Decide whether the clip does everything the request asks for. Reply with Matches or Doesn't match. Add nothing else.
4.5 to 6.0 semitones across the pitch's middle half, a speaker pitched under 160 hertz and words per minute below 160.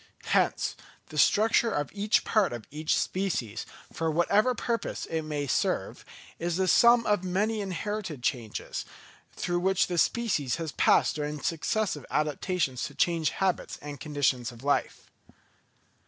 Doesn't match